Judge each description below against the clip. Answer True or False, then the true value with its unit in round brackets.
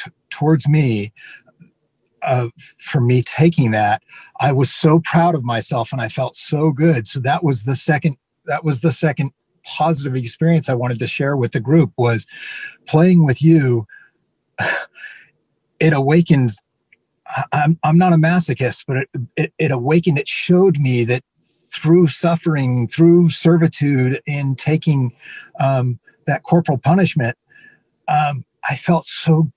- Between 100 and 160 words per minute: True (140 wpm)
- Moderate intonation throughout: True (4.0 semitones)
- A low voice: False (145 Hz)